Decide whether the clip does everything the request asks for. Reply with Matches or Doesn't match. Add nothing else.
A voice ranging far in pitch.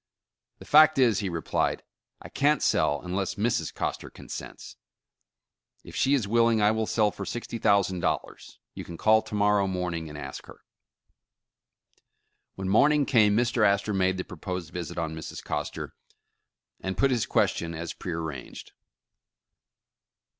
Doesn't match